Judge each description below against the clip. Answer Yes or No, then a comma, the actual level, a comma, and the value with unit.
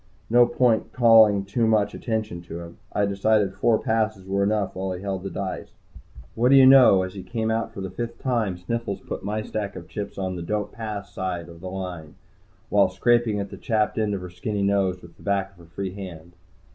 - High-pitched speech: No, low, 100 Hz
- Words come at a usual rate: No, fast, 220 wpm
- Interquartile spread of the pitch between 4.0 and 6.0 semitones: No, average, 3.0 semitones